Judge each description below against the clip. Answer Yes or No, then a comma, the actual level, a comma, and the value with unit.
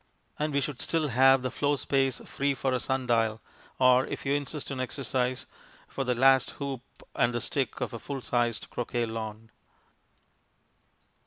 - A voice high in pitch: No, low, 130 Hz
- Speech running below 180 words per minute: Yes, average, 165 wpm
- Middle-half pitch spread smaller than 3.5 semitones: Yes, narrow, 2.4 semitones